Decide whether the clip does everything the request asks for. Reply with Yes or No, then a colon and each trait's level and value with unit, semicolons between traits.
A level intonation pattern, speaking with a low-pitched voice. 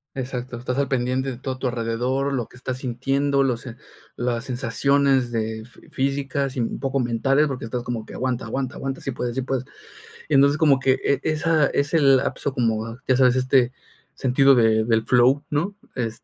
Yes: narrow, 2.1 semitones; low, 130 Hz